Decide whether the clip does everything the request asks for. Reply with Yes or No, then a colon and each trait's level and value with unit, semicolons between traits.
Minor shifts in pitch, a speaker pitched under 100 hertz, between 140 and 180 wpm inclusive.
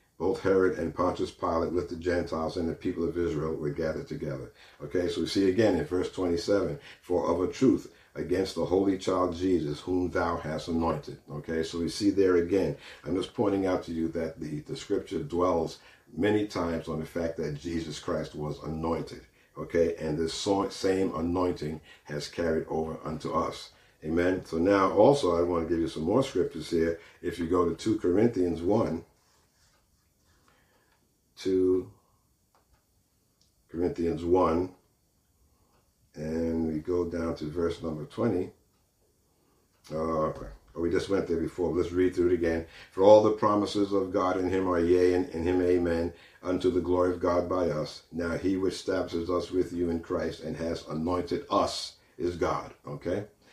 Yes: narrow, 2.0 semitones; very low, 85 Hz; average, 175 wpm